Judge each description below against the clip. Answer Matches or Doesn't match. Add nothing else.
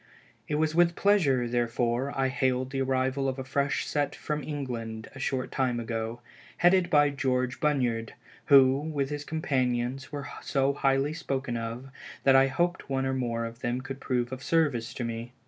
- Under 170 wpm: Doesn't match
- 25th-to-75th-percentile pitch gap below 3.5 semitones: Matches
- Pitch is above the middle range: Doesn't match